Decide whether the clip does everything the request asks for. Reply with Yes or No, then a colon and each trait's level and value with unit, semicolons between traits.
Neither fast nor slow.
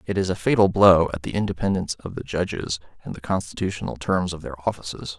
No: fast, 210 wpm